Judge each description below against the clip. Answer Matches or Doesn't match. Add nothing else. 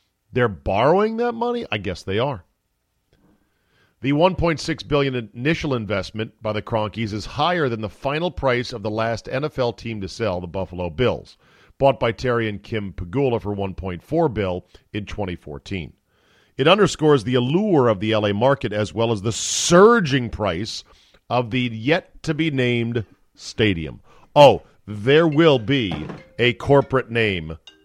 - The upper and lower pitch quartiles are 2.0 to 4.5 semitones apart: Doesn't match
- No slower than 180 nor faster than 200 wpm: Doesn't match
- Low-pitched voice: Matches